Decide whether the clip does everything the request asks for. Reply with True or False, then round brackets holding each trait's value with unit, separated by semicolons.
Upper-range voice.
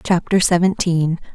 False (175 Hz)